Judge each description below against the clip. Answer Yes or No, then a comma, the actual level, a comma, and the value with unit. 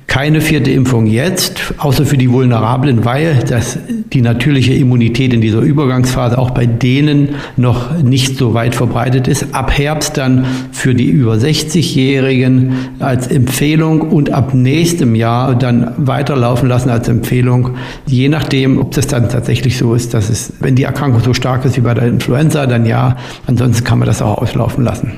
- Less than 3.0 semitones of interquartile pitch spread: Yes, narrow, 2.6 semitones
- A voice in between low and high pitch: No, low, 130 Hz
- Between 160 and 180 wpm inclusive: Yes, average, 170 wpm